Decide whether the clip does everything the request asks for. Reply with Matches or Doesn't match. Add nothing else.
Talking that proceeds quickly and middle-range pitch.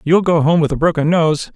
Matches